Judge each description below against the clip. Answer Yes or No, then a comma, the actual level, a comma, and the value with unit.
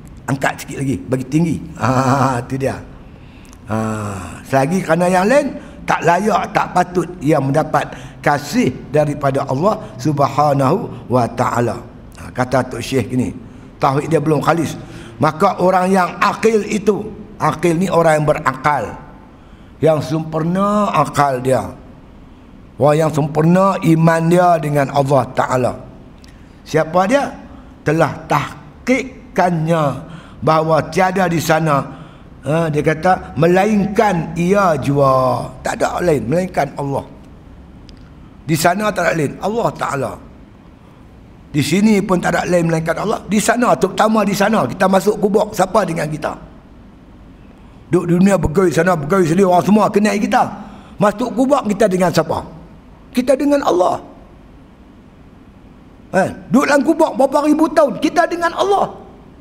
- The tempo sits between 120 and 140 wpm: Yes, average, 130 wpm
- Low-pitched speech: No, medium, 160 Hz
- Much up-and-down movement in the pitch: Yes, wide, 6.4 semitones